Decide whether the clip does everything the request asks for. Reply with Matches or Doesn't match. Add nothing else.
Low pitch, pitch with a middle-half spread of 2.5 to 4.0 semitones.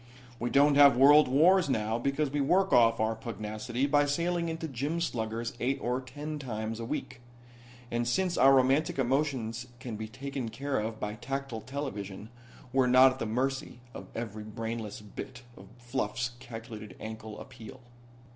Matches